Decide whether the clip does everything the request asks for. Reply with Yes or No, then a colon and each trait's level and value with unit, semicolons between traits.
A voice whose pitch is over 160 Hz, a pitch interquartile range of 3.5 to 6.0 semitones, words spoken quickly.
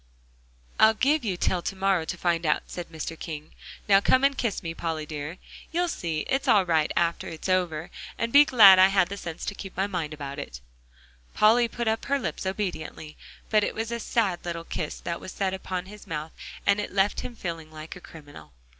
Yes: medium, 185 Hz; average, 4.5 semitones; fast, 215 wpm